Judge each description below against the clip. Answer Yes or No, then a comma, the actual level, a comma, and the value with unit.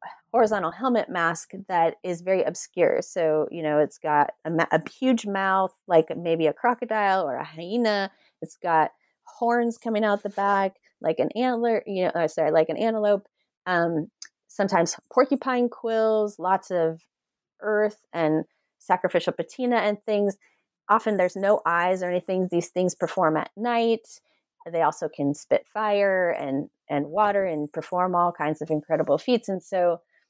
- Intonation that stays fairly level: No, average, 4.5 semitones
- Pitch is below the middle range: No, high, 190 Hz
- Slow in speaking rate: No, average, 155 wpm